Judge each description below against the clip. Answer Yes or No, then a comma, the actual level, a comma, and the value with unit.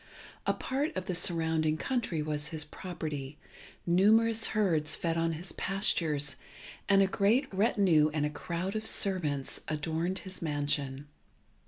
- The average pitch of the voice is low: No, medium, 165 Hz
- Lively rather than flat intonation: No, average, 4.3 semitones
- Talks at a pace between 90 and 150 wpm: Yes, average, 140 wpm